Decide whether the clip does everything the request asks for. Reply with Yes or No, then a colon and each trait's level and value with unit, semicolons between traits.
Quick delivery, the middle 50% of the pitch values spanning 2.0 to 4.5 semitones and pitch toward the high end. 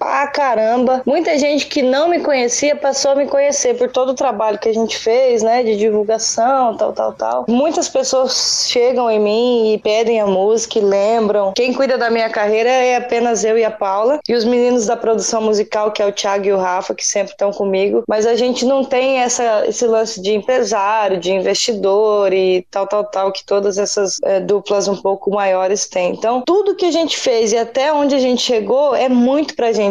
Yes: fast, 215 wpm; average, 4.1 semitones; high, 230 Hz